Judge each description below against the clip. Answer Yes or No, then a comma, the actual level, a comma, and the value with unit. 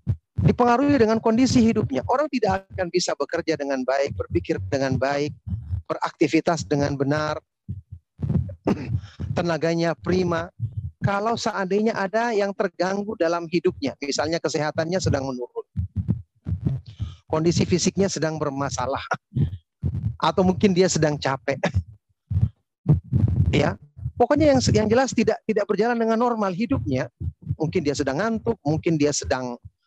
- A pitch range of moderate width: No, wide, 7.6 semitones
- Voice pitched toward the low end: No, medium, 160 Hz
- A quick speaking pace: No, average, 115 wpm